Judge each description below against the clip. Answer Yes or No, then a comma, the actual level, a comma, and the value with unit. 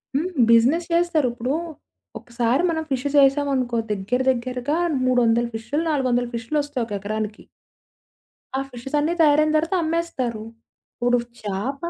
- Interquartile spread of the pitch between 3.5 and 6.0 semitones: Yes, average, 4.0 semitones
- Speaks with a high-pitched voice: Yes, very high, 255 Hz